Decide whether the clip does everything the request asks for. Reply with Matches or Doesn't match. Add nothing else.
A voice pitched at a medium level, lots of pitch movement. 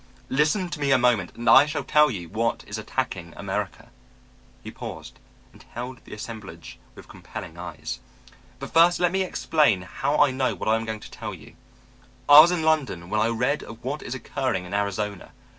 Doesn't match